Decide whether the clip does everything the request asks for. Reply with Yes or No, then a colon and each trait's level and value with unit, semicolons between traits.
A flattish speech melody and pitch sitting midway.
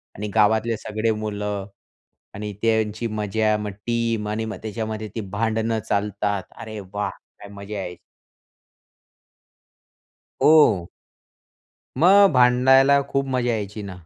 No: narrow, 1.9 semitones; low, 110 Hz